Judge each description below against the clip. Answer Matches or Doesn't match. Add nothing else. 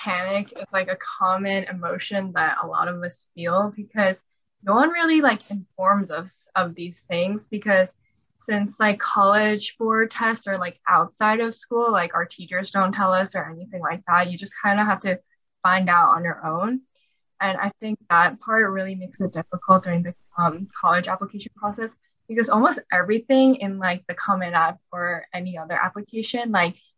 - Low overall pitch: Doesn't match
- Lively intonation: Doesn't match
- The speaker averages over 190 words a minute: Doesn't match